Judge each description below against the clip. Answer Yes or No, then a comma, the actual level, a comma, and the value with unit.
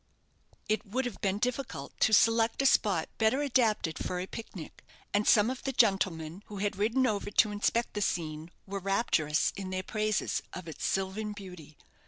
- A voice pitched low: No, high, 205 Hz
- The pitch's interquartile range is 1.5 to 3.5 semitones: Yes, average, 3.2 semitones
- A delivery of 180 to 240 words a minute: Yes, average, 185 wpm